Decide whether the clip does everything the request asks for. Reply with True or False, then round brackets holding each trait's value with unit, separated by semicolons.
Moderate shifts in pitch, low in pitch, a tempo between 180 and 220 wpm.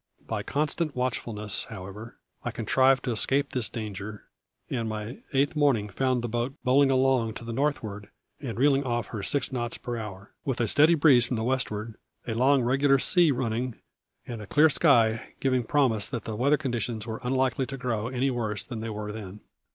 True (3.4 semitones; 120 Hz; 190 wpm)